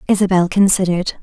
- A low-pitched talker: No, medium, 185 Hz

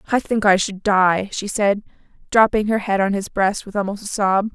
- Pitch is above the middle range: Yes, high, 200 Hz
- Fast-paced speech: Yes, fast, 225 wpm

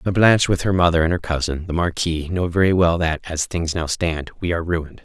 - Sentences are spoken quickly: Yes, fast, 240 wpm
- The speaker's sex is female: No, male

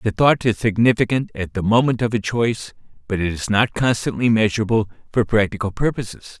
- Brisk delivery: No, average, 180 wpm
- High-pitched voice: No, low, 110 Hz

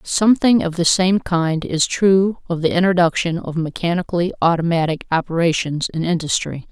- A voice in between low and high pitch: Yes, medium, 170 Hz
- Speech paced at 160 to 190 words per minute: No, average, 145 wpm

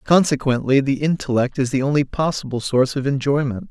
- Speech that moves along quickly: No, average, 160 wpm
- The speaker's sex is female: No, male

